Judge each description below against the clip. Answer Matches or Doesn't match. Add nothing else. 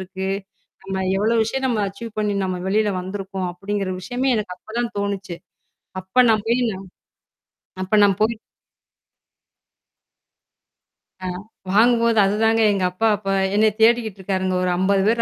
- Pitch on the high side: Matches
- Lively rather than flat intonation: Doesn't match